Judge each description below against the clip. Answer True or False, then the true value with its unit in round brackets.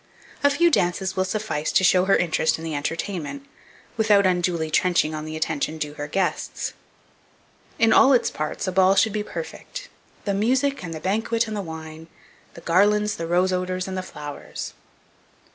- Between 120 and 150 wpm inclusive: False (180 wpm)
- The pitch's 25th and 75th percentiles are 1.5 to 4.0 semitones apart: False (4.6 semitones)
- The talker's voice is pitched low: False (185 Hz)